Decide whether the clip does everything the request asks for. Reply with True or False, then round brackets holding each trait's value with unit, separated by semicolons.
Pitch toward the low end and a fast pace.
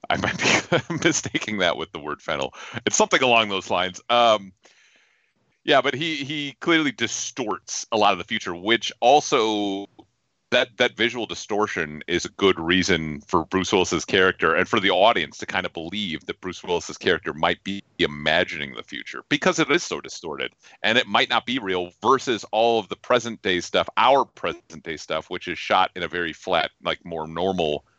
False (105 Hz; 190 wpm)